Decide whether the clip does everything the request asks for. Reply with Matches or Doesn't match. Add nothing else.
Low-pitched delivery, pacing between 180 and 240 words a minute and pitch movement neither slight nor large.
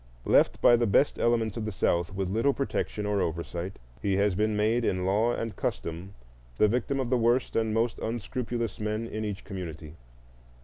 Matches